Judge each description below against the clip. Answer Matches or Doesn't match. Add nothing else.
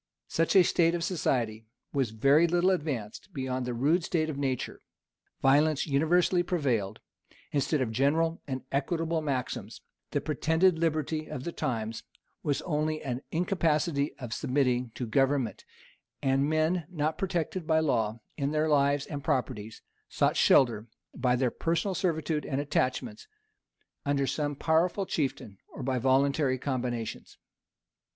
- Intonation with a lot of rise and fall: Doesn't match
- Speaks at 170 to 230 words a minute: Doesn't match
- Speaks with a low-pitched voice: Doesn't match